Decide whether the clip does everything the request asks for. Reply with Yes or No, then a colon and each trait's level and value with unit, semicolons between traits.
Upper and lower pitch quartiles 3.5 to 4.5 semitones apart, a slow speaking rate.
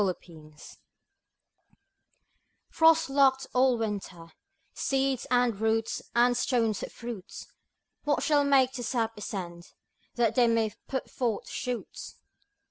Yes: average, 3.8 semitones; slow, 125 wpm